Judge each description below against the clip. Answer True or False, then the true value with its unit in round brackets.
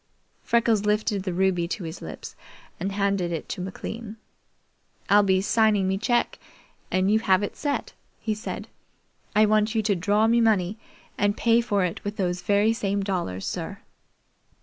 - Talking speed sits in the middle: True (170 wpm)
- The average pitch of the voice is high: True (205 Hz)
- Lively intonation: False (2.5 semitones)